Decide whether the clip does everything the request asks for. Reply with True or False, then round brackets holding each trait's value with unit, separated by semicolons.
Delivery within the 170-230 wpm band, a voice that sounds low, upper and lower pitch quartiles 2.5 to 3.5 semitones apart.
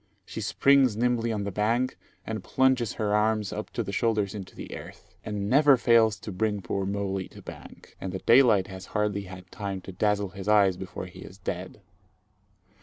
True (190 wpm; 105 Hz; 2.9 semitones)